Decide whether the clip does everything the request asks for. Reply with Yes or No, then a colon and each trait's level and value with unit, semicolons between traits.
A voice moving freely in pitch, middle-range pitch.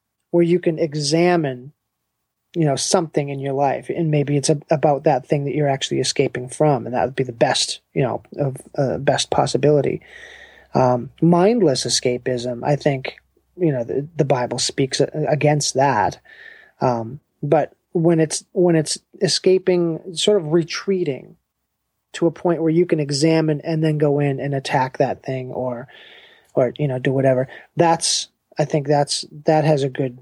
No: average, 3.8 semitones; medium, 150 Hz